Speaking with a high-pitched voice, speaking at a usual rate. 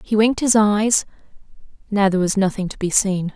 Yes: high, 200 Hz; average, 195 wpm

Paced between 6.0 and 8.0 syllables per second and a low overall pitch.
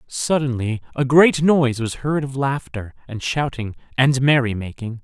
No: 4.6 syllables/s; low, 130 Hz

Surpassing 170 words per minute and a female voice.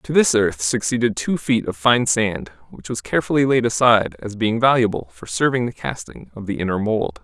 No: fast, 205 wpm; male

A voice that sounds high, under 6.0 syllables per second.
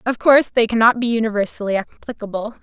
No: high, 225 Hz; 6.5 syllables/s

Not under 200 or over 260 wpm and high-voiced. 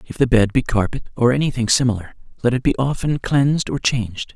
No: fast, 205 wpm; low, 125 Hz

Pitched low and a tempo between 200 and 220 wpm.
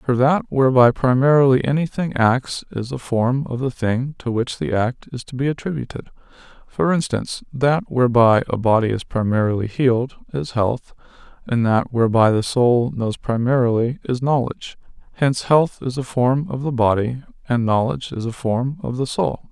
No: low, 125 Hz; average, 170 wpm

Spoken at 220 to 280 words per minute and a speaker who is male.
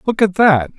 Yes: fast, 230 wpm; male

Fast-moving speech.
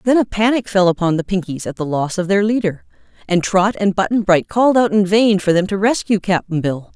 Yes: fast, 240 wpm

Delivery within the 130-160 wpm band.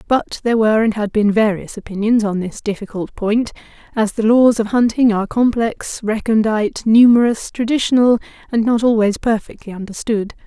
Yes: average, 155 wpm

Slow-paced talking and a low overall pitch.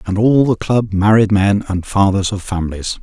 No: average, 200 wpm; low, 100 Hz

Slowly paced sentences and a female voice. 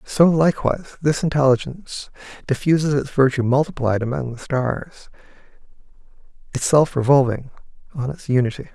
No: slow, 110 wpm; male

